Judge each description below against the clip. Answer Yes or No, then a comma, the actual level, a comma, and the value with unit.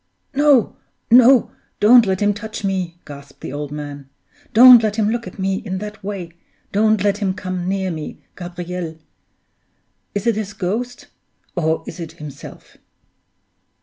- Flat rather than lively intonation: No, average, 3.9 semitones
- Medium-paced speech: Yes, average, 150 wpm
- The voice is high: Yes, high, 195 Hz